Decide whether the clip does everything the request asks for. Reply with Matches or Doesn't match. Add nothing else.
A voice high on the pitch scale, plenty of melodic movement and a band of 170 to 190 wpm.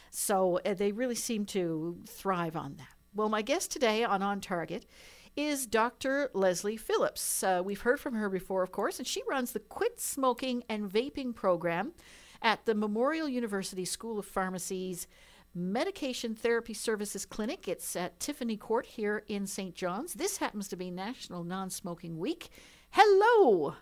Doesn't match